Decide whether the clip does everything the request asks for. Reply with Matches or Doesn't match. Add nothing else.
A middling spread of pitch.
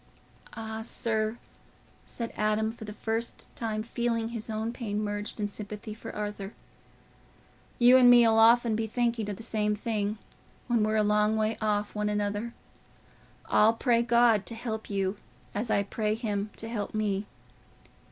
Doesn't match